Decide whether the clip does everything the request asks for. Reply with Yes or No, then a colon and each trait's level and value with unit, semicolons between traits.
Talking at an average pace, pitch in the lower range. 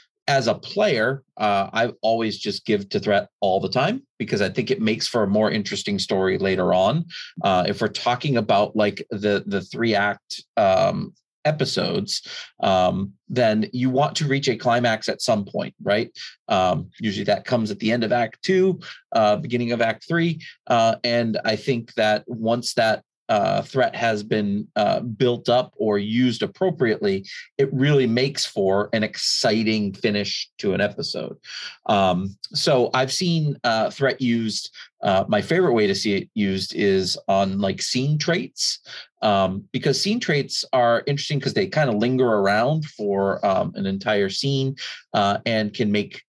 Yes: average, 170 wpm; low, 115 Hz